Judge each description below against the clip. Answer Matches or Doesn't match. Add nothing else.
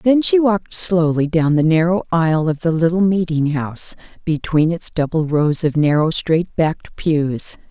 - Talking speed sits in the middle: Matches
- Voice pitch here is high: Doesn't match